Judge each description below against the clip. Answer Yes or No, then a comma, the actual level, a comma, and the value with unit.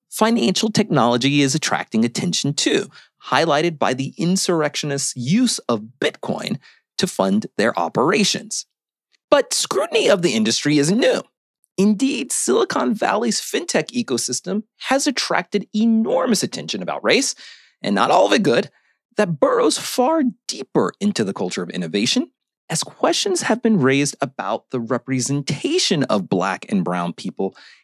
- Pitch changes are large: Yes, wide, 8.4 semitones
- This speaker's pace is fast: No, slow, 135 wpm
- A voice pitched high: Yes, high, 200 Hz